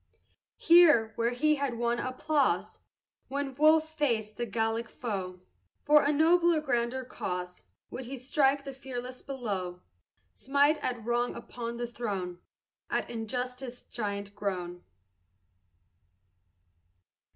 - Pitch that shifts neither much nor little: Yes, average, 4.1 semitones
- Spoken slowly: Yes, slow, 115 wpm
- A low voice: No, high, 245 Hz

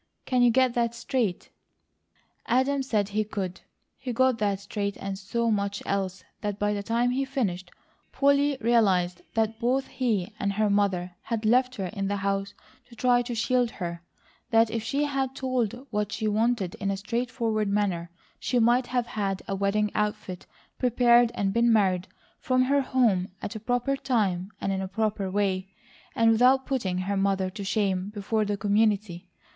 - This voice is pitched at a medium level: No, high, 215 Hz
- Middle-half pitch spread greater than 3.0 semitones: Yes, average, 3.6 semitones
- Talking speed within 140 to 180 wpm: Yes, average, 175 wpm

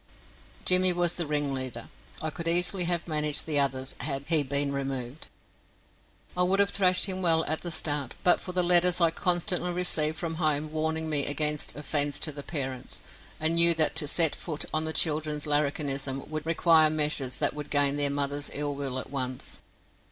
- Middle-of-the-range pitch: Yes, medium, 155 Hz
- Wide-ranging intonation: No, average, 2.9 semitones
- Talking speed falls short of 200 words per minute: Yes, average, 190 wpm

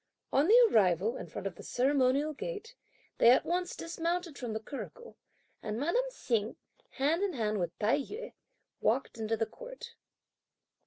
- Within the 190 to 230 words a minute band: No, average, 160 wpm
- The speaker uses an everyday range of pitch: No, wide, 8.7 semitones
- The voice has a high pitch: Yes, very high, 280 Hz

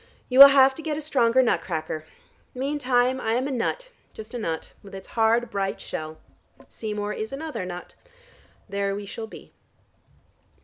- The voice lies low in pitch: No, high, 230 Hz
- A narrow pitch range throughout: No, average, 5.0 semitones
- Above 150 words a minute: Yes, average, 170 wpm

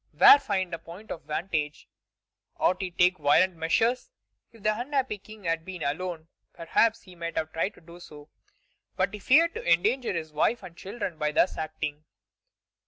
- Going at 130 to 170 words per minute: No, average, 180 wpm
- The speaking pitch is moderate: Yes, medium, 180 Hz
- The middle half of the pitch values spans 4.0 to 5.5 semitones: Yes, average, 4.7 semitones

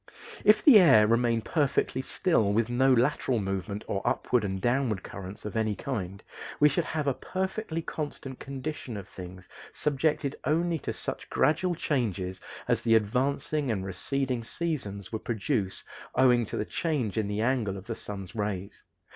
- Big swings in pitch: Yes, wide, 5.9 semitones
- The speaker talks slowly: No, average, 165 wpm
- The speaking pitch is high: No, low, 120 Hz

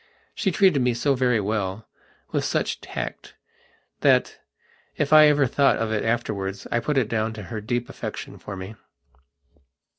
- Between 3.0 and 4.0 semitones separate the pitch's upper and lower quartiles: No, average, 4.4 semitones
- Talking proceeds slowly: No, average, 150 wpm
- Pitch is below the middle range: Yes, low, 115 Hz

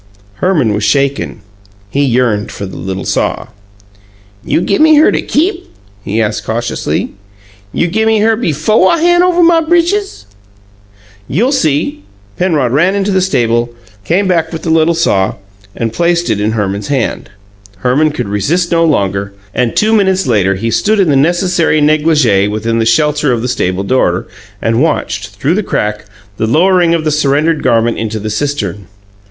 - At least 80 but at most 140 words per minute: No, average, 165 wpm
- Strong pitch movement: Yes, wide, 8.3 semitones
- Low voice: No, medium, 145 Hz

